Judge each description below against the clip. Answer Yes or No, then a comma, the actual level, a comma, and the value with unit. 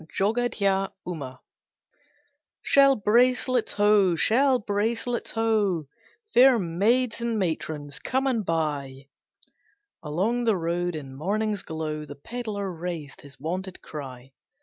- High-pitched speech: Yes, high, 195 Hz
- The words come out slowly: Yes, slow, 110 wpm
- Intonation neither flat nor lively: No, wide, 6.5 semitones